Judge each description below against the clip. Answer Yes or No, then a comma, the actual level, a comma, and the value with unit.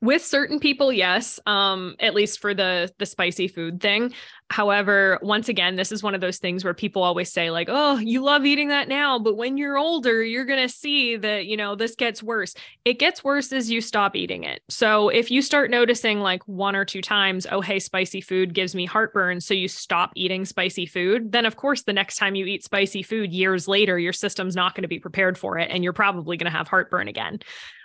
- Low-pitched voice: No, high, 205 Hz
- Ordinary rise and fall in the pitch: Yes, average, 4.3 semitones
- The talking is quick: Yes, fast, 225 wpm